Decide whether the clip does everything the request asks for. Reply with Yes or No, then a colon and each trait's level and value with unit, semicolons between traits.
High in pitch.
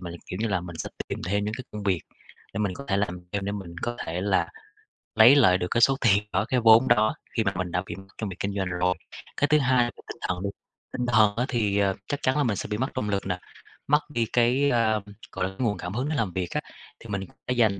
No: low, 105 Hz